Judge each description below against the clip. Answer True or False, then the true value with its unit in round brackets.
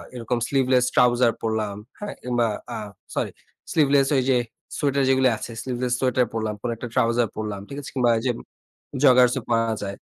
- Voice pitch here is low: True (125 Hz)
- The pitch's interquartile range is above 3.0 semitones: False (2.4 semitones)